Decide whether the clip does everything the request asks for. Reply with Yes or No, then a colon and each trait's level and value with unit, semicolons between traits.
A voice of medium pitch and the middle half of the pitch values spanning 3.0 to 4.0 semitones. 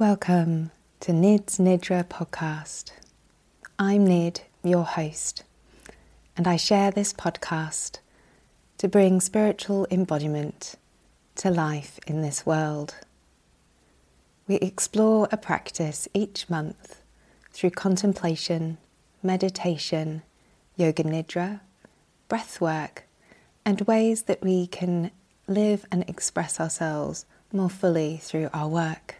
Yes: medium, 175 Hz; average, 3.5 semitones